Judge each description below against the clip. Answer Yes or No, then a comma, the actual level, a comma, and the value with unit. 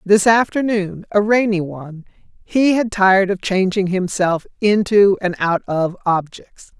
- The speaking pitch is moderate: No, high, 195 Hz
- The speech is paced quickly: No, average, 140 wpm